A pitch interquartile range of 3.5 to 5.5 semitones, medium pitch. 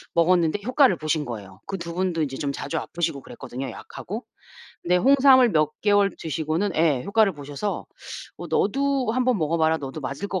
Yes: average, 5.2 semitones; medium, 170 Hz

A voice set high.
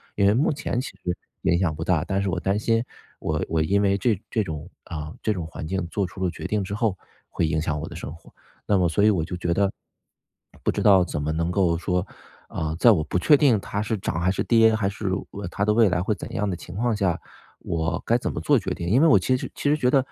No: very low, 95 Hz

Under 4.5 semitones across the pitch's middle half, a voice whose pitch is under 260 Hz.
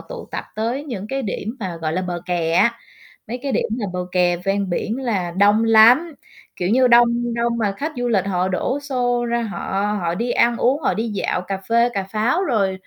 Yes: average, 4.1 semitones; high, 220 Hz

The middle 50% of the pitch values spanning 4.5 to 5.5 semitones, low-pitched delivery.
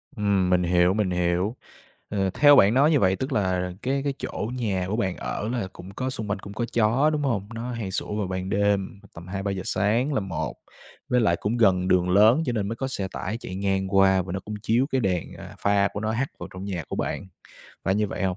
No: average, 3.7 semitones; low, 100 Hz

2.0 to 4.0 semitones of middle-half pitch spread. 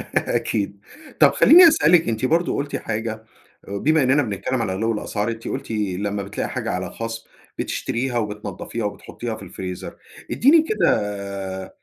No: average, 4.5 semitones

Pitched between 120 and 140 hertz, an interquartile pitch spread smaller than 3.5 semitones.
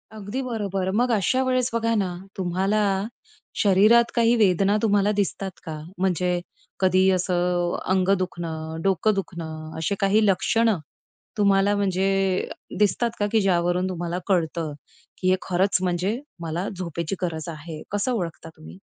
No: high, 190 Hz; average, 2.9 semitones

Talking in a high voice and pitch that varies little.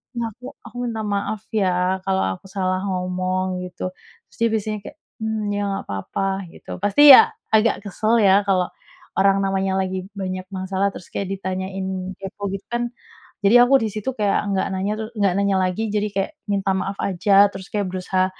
Yes: high, 195 Hz; narrow, 2.2 semitones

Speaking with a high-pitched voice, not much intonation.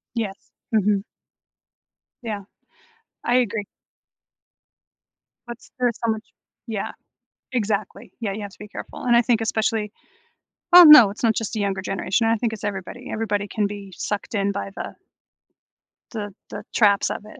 Yes: high, 215 Hz; narrow, 2.2 semitones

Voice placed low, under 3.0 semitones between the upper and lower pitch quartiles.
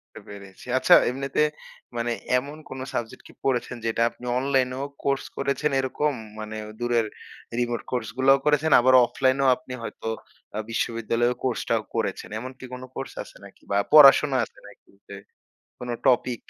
Yes: low, 130 Hz; narrow, 2.4 semitones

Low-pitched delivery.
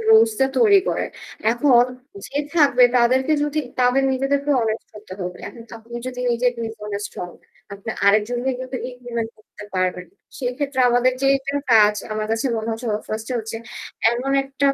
No: high, 240 Hz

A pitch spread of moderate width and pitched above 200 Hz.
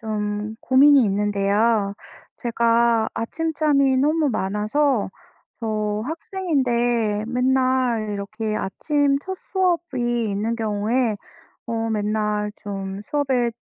Yes: average, 4.3 semitones; high, 230 Hz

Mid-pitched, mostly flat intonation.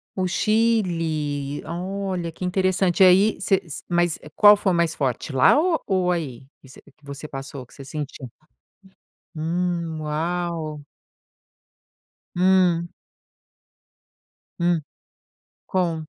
No: medium, 170 Hz; average, 3.4 semitones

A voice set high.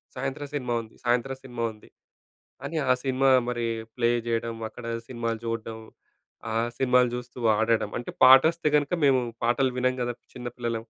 No: low, 125 Hz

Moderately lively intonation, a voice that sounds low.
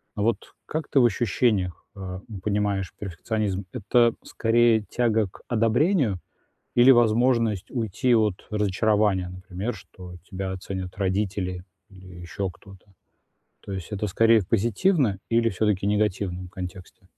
Yes: average, 3.4 semitones; low, 105 Hz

